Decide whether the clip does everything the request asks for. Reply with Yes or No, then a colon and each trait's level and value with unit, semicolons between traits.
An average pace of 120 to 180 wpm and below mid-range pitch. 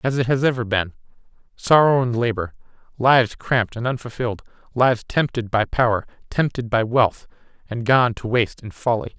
Yes: average, 155 wpm; low, 120 Hz